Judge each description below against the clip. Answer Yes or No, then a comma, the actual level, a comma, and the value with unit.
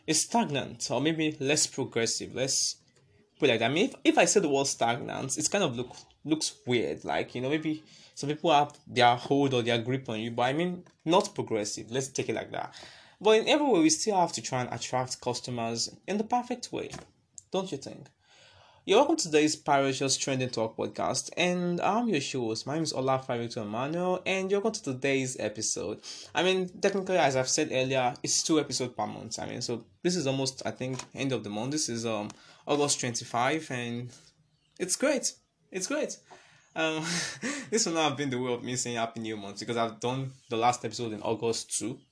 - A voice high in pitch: No, low, 135 Hz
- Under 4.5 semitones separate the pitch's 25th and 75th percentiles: No, average, 5.0 semitones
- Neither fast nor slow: No, fast, 220 wpm